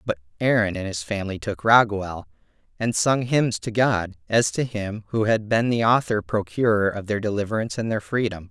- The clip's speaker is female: No, male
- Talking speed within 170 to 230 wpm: Yes, average, 190 wpm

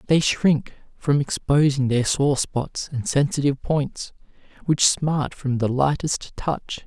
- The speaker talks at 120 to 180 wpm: Yes, average, 140 wpm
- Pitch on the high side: No, medium, 140 Hz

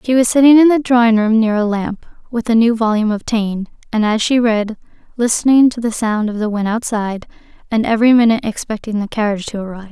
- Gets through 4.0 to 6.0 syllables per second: No, 6.5 syllables/s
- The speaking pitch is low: No, high, 225 Hz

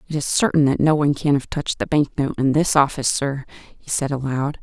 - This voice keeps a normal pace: No, fast, 245 wpm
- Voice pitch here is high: No, medium, 140 Hz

